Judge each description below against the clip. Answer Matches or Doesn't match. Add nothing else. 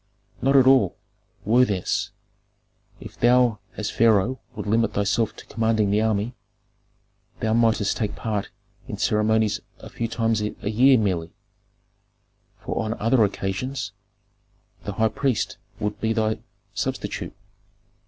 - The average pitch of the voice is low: Matches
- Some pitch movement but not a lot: Doesn't match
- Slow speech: Matches